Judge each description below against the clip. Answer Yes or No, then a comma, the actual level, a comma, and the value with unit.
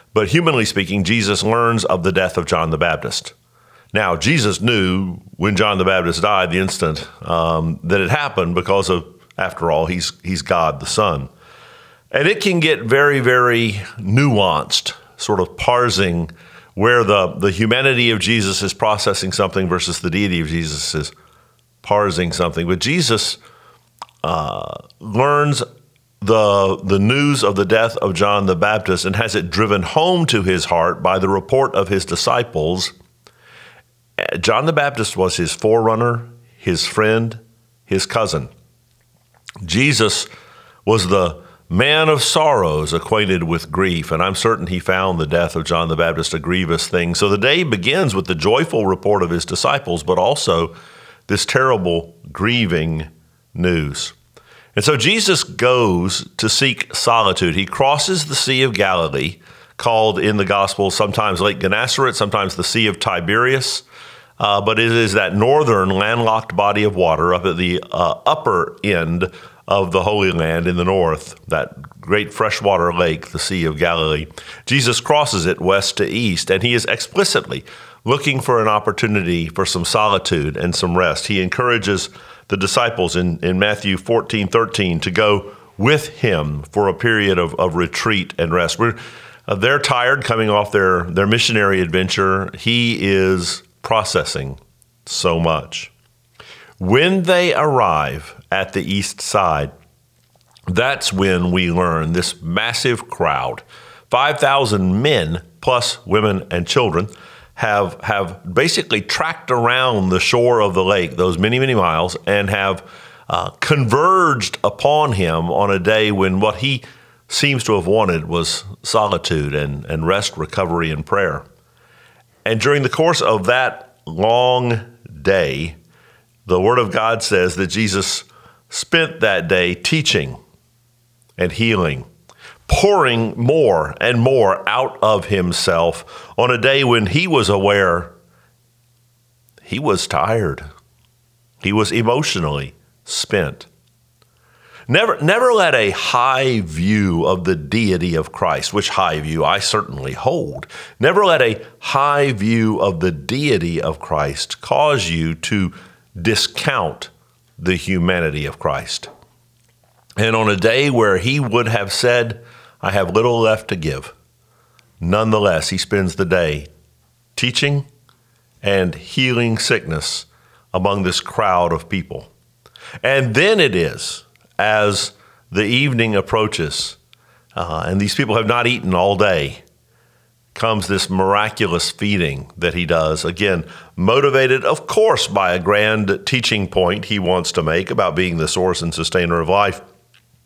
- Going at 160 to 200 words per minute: No, average, 145 wpm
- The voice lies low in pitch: Yes, low, 100 Hz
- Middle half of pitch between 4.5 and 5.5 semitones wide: Yes, average, 4.8 semitones